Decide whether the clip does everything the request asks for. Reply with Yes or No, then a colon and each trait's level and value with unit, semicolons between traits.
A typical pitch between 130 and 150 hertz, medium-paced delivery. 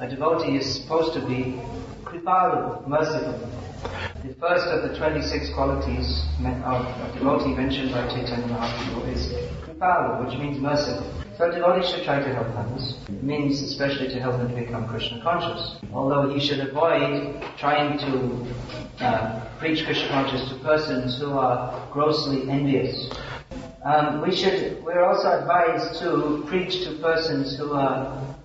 Yes: low, 135 Hz; average, 150 wpm